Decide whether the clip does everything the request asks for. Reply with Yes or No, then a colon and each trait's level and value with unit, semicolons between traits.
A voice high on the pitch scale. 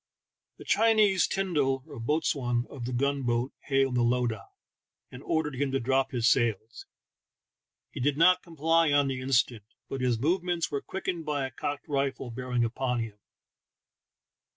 No: low, 135 Hz